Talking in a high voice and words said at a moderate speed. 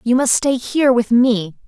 Yes: high, 245 Hz; average, 180 wpm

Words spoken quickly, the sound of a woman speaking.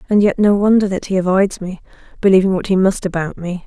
Yes: fast, 230 wpm; female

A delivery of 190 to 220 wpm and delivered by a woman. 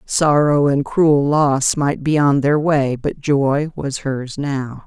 No: average, 175 wpm; female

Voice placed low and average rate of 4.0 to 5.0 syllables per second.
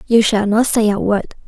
No: high, 215 Hz; 4.9 syllables/s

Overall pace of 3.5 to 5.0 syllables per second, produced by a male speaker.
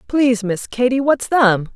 No: 4.4 syllables/s; female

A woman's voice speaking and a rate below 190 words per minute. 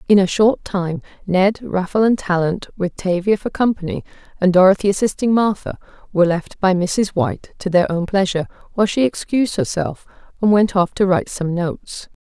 Yes: female; average, 175 wpm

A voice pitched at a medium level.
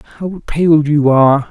Yes: medium, 150 Hz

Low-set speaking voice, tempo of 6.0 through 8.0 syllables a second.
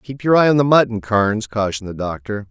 Yes: low, 115 Hz; 6.1 syllables/s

